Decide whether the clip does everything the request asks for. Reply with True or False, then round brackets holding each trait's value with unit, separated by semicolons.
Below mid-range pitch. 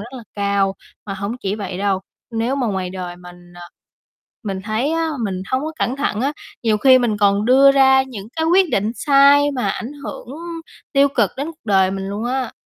False (225 Hz)